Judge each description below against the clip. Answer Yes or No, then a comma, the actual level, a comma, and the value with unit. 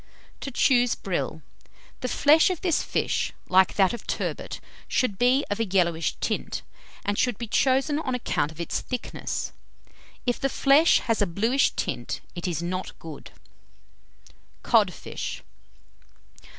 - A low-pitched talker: No, high, 230 Hz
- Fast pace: No, average, 140 wpm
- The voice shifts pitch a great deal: Yes, wide, 6.3 semitones